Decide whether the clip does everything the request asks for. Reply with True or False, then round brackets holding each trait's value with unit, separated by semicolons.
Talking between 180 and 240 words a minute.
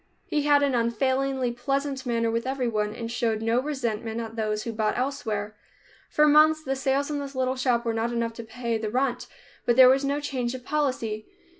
True (200 wpm)